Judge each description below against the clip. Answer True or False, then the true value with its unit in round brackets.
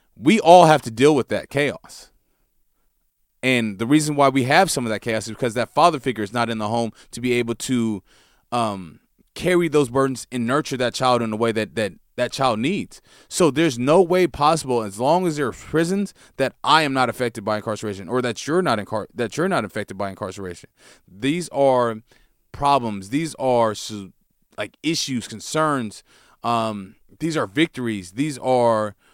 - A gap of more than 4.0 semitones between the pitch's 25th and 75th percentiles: True (4.9 semitones)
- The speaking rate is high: False (190 wpm)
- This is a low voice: True (125 Hz)